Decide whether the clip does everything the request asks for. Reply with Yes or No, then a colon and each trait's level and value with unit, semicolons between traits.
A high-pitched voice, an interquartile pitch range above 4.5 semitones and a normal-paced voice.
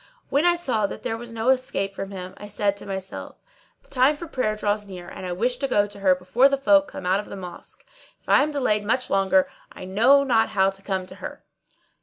No: high, 210 Hz; average, 4.9 semitones; fast, 245 wpm